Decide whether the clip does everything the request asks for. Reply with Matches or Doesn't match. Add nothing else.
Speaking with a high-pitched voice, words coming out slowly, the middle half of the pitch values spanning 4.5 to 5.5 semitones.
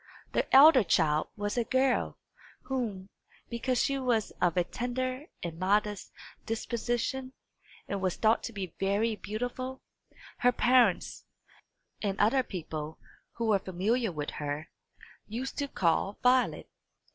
Matches